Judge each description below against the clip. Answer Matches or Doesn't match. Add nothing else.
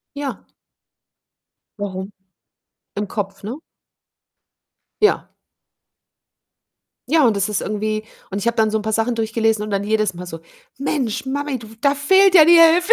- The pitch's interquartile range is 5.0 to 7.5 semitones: Matches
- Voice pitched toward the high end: Matches